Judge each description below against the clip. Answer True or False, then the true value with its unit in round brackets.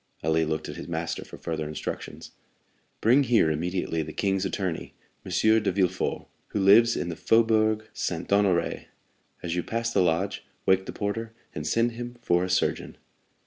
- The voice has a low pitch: True (95 Hz)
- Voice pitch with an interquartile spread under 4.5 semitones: False (4.8 semitones)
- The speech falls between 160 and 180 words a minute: True (170 wpm)